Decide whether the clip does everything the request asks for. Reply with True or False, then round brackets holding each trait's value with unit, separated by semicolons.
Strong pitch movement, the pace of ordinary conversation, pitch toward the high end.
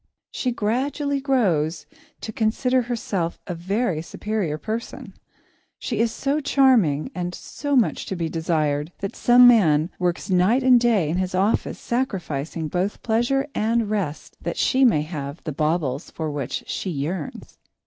True (7.0 semitones; 150 wpm; 195 Hz)